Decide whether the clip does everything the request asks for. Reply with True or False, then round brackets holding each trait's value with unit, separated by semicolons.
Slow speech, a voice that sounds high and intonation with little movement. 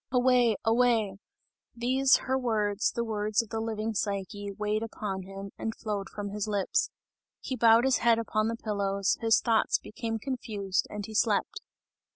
False (165 wpm; 220 Hz; 2.2 semitones)